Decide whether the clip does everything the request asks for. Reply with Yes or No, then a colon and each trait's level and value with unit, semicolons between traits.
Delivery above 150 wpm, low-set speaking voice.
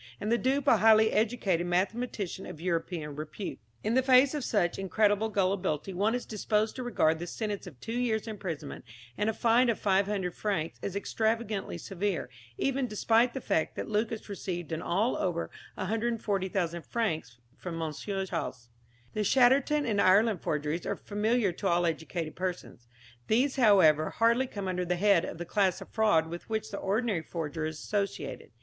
No: average, 170 wpm; high, 200 Hz